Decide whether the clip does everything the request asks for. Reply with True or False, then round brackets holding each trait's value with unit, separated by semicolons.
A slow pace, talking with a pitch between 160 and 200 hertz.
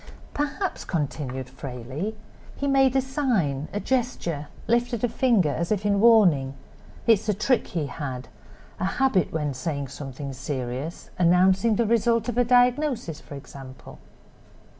True (125 wpm; 185 Hz)